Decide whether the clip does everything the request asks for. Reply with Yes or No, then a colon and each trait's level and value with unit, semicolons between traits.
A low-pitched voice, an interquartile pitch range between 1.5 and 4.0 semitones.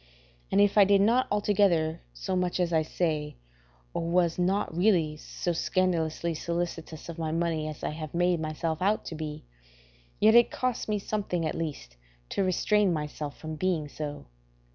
No: medium, 170 Hz; average, 3.4 semitones